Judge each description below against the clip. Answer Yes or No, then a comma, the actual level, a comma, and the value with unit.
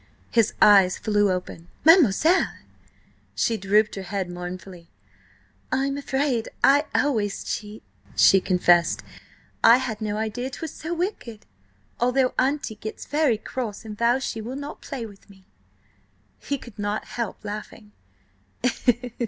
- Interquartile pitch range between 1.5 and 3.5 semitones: No, average, 4.7 semitones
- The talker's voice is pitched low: No, high, 220 Hz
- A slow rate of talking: Yes, slow, 130 wpm